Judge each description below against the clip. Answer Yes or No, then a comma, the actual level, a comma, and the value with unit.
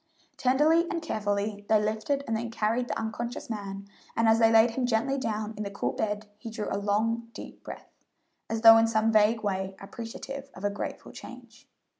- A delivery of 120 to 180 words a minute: No, average, 195 wpm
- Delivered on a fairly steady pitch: Yes, narrow, 2.2 semitones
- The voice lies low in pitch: No, high, 225 Hz